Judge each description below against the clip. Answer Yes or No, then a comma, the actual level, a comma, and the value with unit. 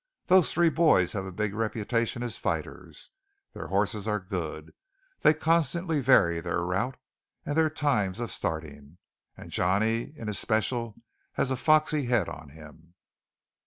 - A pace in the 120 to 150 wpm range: Yes, average, 145 wpm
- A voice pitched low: Yes, low, 110 Hz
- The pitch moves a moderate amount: No, wide, 7.6 semitones